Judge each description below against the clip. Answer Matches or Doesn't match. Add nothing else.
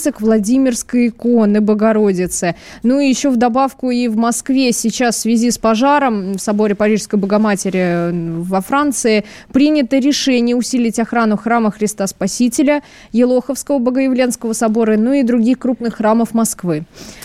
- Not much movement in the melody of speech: Doesn't match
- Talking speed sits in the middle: Matches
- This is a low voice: Doesn't match